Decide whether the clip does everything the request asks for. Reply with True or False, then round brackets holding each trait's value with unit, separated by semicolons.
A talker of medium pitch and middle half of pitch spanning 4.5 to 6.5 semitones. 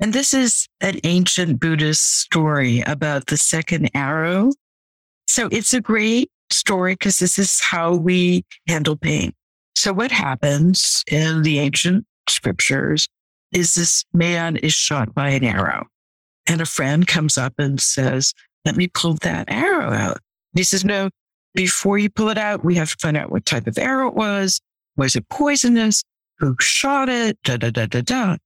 True (170 Hz; 5.4 semitones)